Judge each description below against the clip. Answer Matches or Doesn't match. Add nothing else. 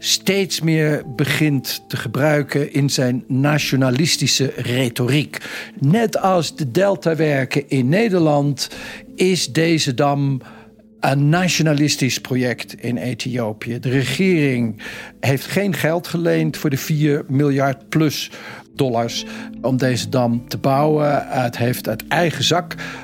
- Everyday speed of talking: Doesn't match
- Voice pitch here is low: Doesn't match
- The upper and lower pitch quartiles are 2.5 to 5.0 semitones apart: Matches